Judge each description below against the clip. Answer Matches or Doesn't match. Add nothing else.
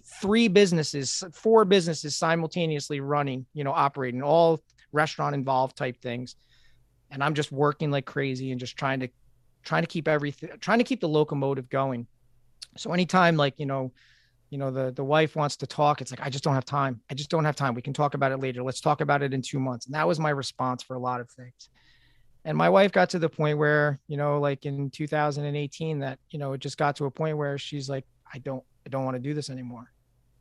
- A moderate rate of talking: Doesn't match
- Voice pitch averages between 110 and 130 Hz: Doesn't match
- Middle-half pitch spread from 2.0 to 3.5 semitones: Matches